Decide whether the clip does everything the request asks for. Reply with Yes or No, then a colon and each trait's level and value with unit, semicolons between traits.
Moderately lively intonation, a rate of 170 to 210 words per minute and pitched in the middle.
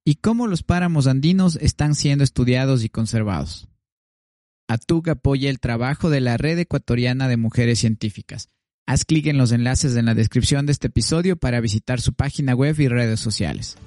No: average, 4.2 semitones; average, 175 wpm; low, 125 Hz